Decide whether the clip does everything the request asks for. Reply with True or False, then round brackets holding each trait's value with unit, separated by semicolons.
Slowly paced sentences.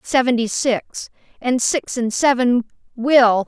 True (120 wpm)